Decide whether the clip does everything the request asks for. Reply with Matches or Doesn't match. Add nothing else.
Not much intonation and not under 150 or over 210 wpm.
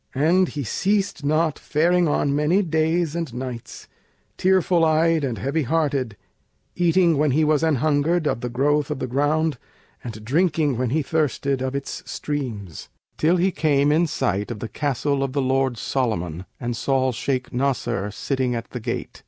Doesn't match